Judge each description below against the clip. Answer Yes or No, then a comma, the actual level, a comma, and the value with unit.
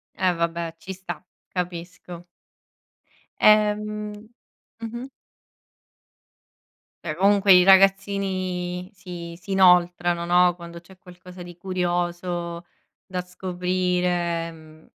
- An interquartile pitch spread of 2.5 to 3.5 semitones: No, narrow, 1.6 semitones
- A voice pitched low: No, medium, 180 Hz